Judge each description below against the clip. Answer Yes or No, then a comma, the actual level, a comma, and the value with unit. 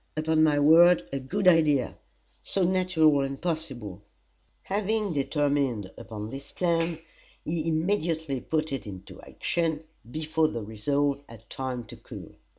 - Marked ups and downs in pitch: No, average, 3.6 semitones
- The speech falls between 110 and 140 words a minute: Yes, slow, 135 wpm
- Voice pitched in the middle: Yes, medium, 155 Hz